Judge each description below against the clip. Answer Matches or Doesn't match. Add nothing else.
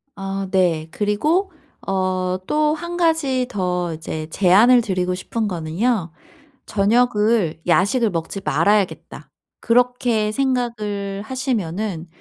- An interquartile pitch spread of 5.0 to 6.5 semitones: Matches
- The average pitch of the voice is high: Matches